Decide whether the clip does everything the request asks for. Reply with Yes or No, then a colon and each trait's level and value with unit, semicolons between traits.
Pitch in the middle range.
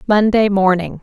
No: high, 200 Hz